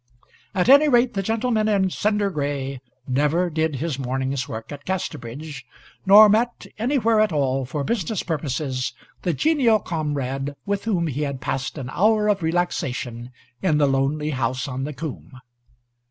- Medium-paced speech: Yes, average, 155 wpm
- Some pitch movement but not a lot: No, wide, 7.3 semitones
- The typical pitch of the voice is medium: Yes, medium, 155 Hz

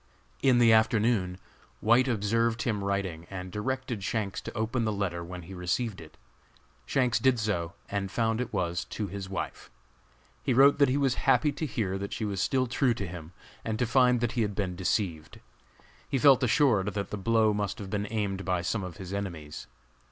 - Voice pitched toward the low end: Yes, low, 105 Hz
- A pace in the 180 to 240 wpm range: Yes, average, 195 wpm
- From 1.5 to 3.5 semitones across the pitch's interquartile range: No, average, 3.9 semitones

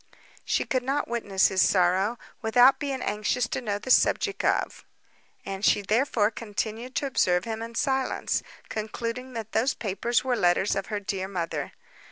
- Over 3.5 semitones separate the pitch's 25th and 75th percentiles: Yes, average, 4.0 semitones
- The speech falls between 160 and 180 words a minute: Yes, average, 165 wpm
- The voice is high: Yes, high, 220 Hz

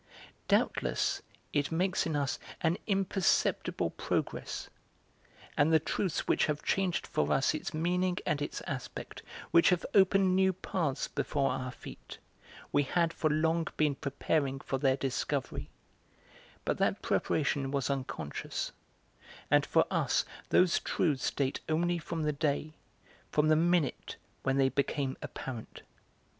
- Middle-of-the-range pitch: Yes, medium, 155 Hz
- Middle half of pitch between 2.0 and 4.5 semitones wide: Yes, average, 3.9 semitones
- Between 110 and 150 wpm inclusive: Yes, slow, 135 wpm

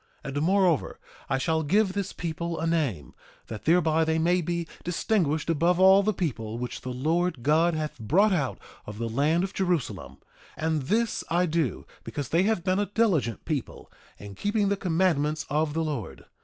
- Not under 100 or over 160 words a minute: No, average, 185 wpm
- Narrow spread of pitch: No, average, 3.9 semitones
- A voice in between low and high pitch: Yes, medium, 165 Hz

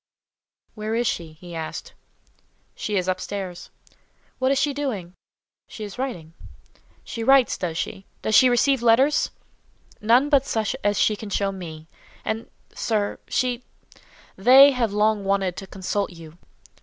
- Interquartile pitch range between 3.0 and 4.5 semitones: No, average, 5.0 semitones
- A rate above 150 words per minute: No, average, 140 wpm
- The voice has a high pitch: Yes, high, 210 Hz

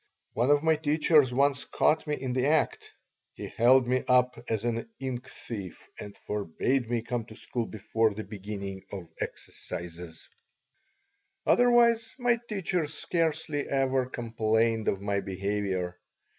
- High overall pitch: No, low, 120 Hz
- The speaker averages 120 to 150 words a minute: Yes, average, 140 wpm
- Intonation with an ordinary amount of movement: No, wide, 5.8 semitones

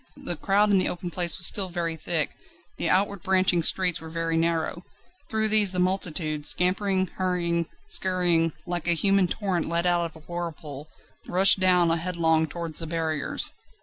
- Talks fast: No, average, 170 wpm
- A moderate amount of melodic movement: No, narrow, 2.2 semitones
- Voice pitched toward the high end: No, medium, 175 Hz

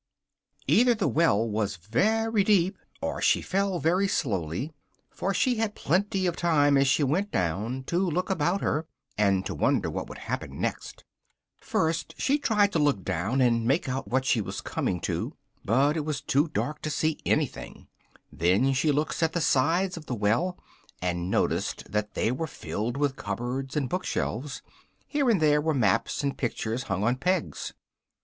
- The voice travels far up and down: Yes, wide, 7.5 semitones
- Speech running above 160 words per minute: Yes, average, 180 wpm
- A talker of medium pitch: Yes, medium, 145 Hz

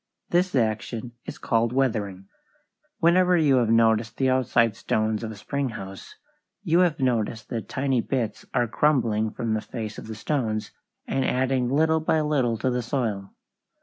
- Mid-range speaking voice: No, low, 120 Hz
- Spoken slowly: No, average, 165 wpm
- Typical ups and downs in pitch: Yes, average, 3.6 semitones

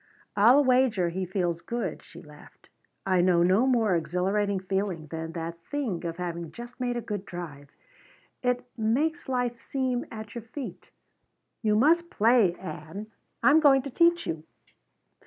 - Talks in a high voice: Yes, high, 210 Hz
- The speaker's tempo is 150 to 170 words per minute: Yes, average, 155 wpm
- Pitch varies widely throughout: Yes, wide, 6.1 semitones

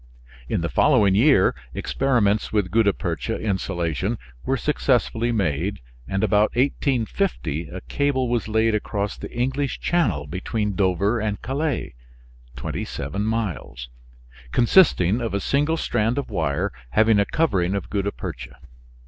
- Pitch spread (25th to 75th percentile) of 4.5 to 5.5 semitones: Yes, average, 5.0 semitones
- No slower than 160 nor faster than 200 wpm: No, slow, 135 wpm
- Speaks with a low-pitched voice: Yes, low, 105 Hz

